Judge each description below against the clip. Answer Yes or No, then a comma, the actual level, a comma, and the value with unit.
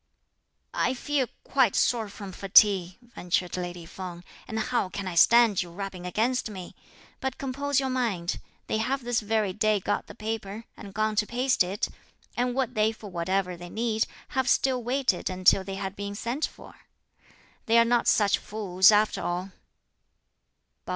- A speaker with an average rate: Yes, average, 165 wpm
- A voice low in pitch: No, high, 215 Hz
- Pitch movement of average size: Yes, average, 4.3 semitones